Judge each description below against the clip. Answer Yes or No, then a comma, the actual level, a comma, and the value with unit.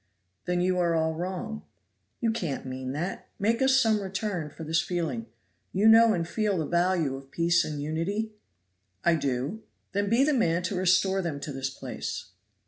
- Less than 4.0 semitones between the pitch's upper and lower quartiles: No, average, 4.5 semitones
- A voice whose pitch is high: No, medium, 175 Hz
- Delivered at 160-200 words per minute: Yes, average, 180 wpm